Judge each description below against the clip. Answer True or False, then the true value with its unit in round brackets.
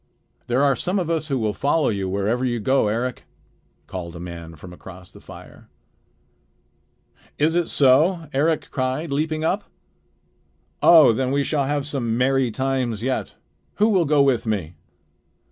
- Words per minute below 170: True (160 wpm)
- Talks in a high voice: False (130 Hz)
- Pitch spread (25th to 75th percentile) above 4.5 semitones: True (5.6 semitones)